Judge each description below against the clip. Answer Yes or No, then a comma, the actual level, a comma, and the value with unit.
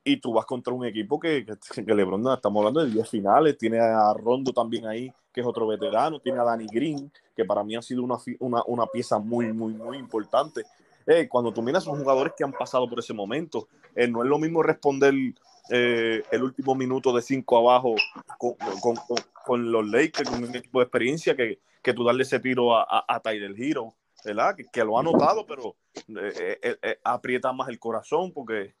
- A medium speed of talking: No, fast, 215 wpm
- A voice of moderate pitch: No, low, 125 Hz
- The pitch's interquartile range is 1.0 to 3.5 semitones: Yes, average, 2.8 semitones